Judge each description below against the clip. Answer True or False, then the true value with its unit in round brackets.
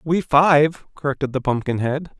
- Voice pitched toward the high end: False (145 Hz)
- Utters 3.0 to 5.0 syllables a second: True (4.5 syllables/s)